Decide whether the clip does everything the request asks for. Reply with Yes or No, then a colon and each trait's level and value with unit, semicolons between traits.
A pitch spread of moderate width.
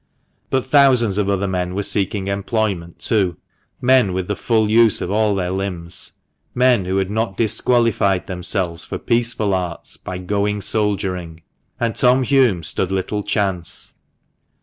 Yes: average, 3.5 semitones